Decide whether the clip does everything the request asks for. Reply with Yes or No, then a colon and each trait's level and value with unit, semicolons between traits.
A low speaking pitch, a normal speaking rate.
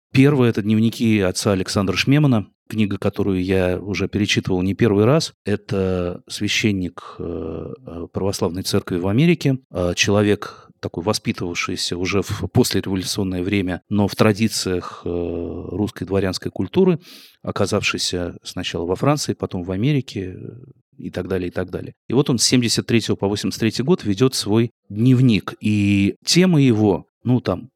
Yes: low, 105 Hz; average, 135 wpm